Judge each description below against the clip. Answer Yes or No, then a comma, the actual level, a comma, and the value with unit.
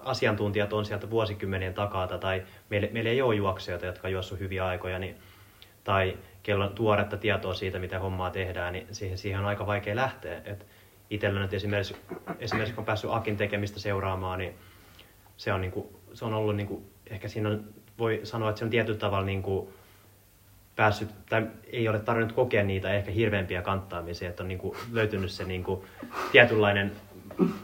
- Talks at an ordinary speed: No, fast, 180 wpm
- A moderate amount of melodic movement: No, narrow, 2.0 semitones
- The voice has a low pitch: Yes, low, 100 Hz